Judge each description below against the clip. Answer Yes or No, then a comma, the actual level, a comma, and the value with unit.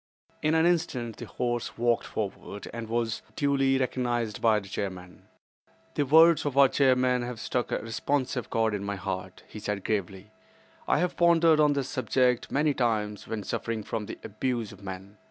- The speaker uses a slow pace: No, average, 175 wpm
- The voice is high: No, low, 120 Hz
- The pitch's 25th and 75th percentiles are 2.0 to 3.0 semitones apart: No, average, 4.4 semitones